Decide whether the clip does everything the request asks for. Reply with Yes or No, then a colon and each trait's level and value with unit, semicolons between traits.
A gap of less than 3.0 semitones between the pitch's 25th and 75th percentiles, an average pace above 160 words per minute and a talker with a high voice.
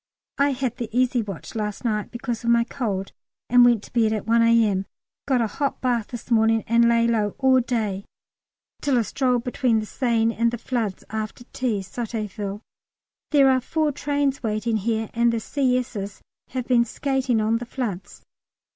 Yes: narrow, 2.5 semitones; average, 180 wpm; high, 235 Hz